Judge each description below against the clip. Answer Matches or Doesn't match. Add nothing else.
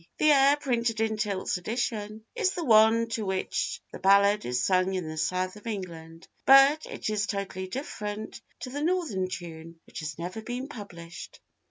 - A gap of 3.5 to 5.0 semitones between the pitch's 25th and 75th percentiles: Matches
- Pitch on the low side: Doesn't match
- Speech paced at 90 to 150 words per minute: Doesn't match